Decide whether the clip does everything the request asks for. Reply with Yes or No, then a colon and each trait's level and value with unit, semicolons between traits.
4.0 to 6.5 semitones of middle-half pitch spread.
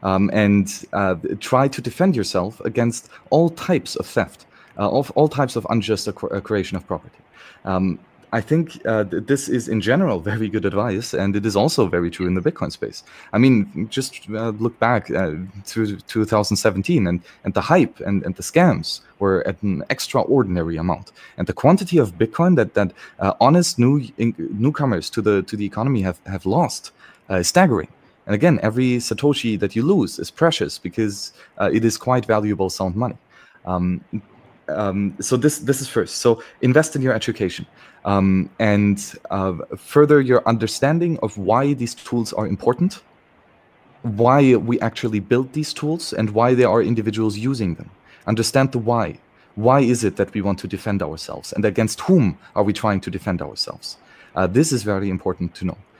Yes: average, 4.3 semitones